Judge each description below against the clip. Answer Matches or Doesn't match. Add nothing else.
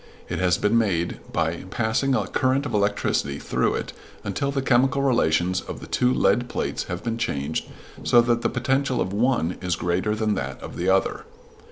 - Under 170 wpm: Doesn't match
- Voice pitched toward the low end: Matches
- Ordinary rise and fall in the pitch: Doesn't match